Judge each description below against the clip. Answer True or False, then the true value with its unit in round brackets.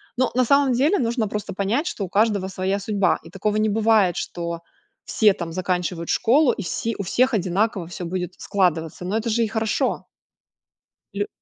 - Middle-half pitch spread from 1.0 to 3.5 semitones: False (3.9 semitones)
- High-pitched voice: True (205 Hz)